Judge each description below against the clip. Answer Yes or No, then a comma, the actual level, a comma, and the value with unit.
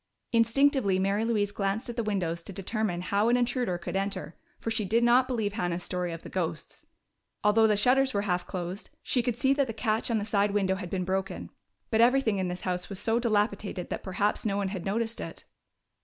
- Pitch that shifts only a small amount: No, average, 3.5 semitones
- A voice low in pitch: No, high, 205 Hz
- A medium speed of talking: No, fast, 215 wpm